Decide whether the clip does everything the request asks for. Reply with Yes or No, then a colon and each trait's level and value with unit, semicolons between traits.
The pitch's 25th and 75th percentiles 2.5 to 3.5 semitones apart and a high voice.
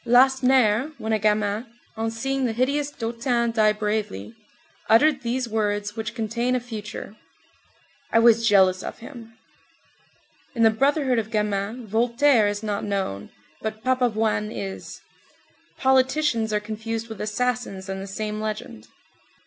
Yes: average, 2.8 semitones; high, 225 Hz